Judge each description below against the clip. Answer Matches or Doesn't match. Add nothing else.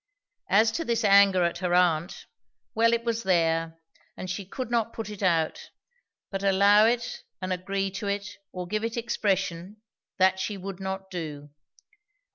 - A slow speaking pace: Doesn't match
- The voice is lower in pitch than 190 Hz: Doesn't match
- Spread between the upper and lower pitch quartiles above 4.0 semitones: Doesn't match